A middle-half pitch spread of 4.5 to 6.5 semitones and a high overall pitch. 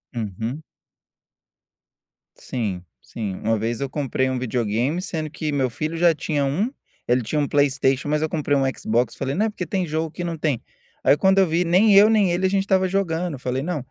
No: wide, 5.6 semitones; medium, 150 Hz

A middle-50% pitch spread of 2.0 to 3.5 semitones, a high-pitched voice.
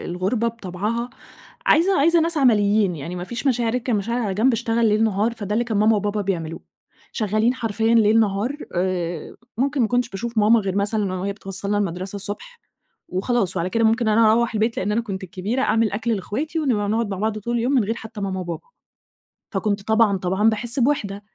Yes: average, 3.0 semitones; high, 215 Hz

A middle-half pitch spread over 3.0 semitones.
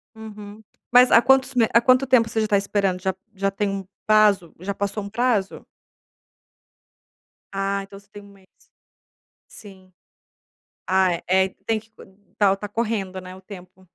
No: narrow, 2.4 semitones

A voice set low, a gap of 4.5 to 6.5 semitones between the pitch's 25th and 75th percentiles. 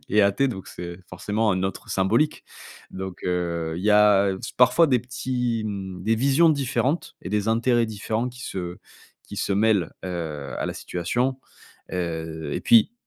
Yes: low, 105 Hz; average, 5.2 semitones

